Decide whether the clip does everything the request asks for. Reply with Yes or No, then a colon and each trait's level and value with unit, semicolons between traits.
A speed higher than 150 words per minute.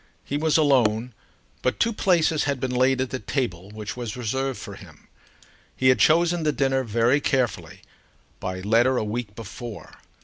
Yes: average, 170 wpm